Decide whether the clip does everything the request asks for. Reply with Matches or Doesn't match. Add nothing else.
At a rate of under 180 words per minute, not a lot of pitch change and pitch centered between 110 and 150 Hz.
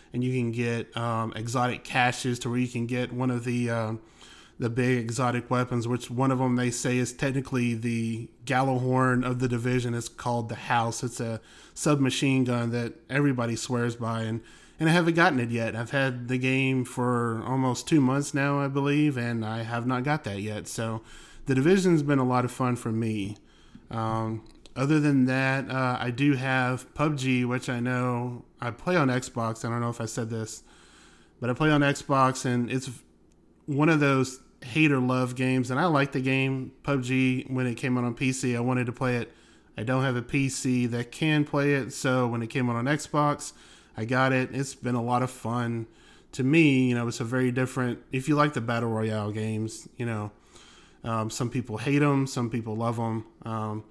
Doesn't match